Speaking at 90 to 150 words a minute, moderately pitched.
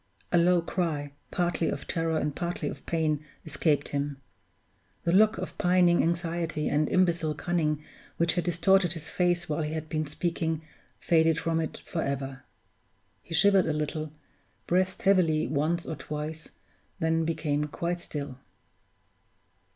Yes: average, 145 wpm; medium, 160 Hz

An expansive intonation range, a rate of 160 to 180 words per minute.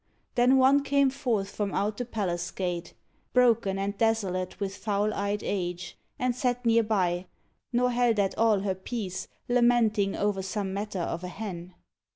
No: average, 3.9 semitones; average, 170 wpm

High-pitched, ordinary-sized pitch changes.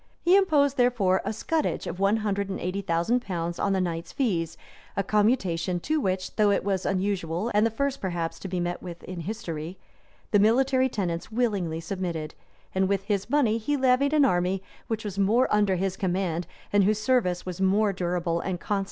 Yes: high, 195 Hz; average, 3.9 semitones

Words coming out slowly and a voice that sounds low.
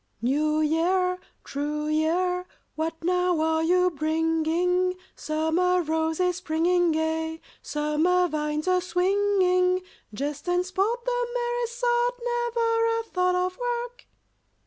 No: slow, 115 wpm; very high, 360 Hz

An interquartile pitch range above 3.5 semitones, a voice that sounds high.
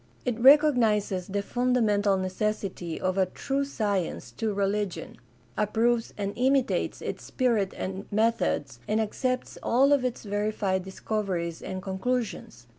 Yes: average, 4.2 semitones; high, 210 Hz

